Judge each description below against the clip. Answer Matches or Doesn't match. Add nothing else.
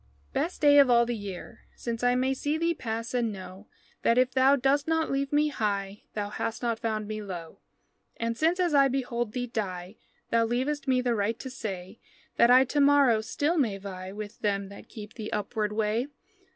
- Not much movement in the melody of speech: Doesn't match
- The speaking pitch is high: Matches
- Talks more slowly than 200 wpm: Doesn't match